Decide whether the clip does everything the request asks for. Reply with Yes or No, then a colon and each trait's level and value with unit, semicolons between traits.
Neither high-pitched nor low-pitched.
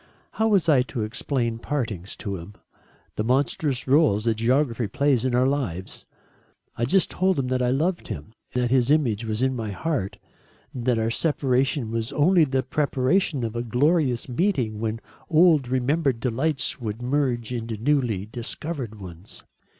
No: low, 125 Hz